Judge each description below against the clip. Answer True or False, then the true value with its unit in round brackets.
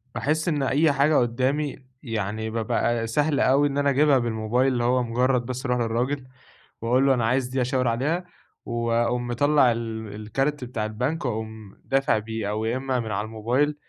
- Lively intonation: False (3.2 semitones)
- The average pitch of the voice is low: True (125 Hz)